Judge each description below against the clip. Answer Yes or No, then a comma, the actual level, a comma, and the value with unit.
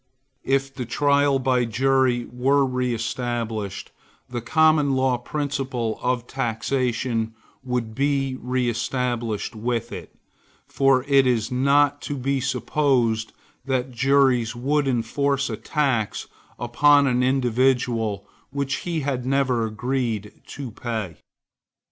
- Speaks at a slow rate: Yes, slow, 110 wpm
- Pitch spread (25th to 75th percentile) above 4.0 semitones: No, average, 2.7 semitones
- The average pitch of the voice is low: Yes, low, 125 Hz